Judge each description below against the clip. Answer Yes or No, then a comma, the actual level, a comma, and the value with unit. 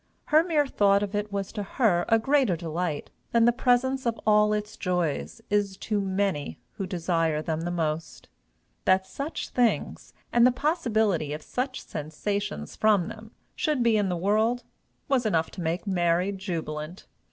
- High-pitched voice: Yes, high, 200 Hz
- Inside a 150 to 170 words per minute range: Yes, average, 165 wpm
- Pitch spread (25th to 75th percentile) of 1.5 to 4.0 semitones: No, average, 5.1 semitones